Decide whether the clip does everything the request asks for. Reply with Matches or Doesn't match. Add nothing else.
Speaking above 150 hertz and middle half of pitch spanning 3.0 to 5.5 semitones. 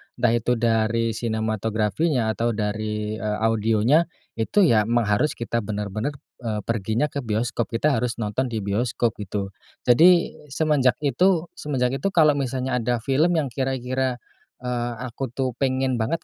Doesn't match